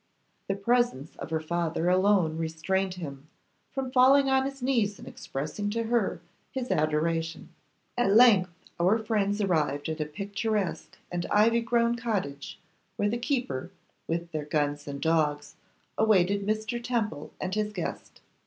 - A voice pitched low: No, high, 195 Hz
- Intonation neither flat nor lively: No, wide, 6.2 semitones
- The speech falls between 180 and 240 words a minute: No, average, 145 wpm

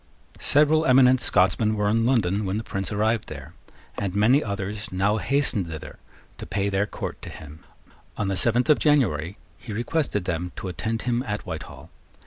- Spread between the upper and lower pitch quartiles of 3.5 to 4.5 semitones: Yes, average, 3.9 semitones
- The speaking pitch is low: Yes, low, 105 Hz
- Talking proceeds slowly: No, average, 175 wpm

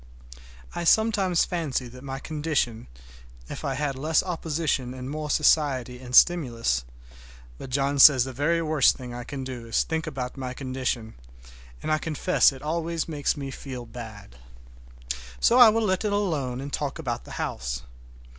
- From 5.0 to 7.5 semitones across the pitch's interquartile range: No, average, 4.4 semitones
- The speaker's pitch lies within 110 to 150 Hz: Yes, low, 135 Hz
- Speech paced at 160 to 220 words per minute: Yes, average, 170 wpm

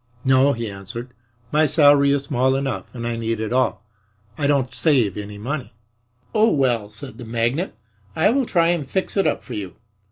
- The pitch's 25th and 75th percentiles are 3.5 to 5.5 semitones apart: Yes, average, 4.1 semitones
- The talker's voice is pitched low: Yes, low, 130 Hz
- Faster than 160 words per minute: Yes, average, 190 wpm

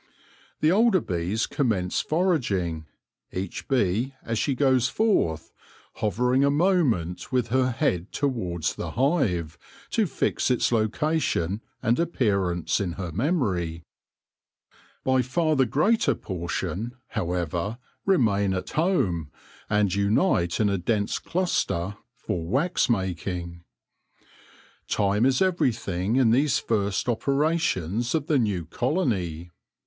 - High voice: No, low, 110 Hz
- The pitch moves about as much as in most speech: No, wide, 7.5 semitones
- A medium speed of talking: No, slow, 120 wpm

